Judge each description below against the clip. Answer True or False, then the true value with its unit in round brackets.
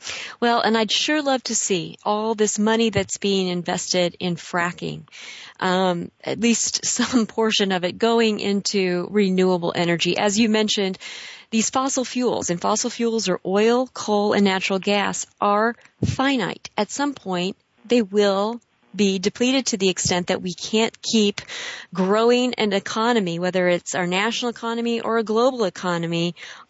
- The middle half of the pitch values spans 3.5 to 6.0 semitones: True (3.9 semitones)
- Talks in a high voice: True (210 Hz)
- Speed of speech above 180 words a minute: False (155 wpm)